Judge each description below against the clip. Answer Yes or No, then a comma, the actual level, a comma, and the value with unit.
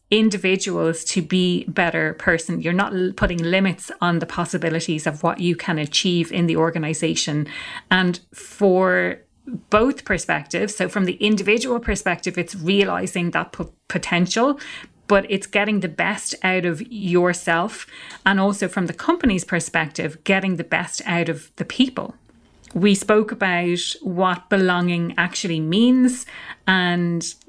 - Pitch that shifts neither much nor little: Yes, average, 3.0 semitones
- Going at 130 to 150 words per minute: Yes, average, 140 wpm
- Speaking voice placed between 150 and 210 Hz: Yes, medium, 185 Hz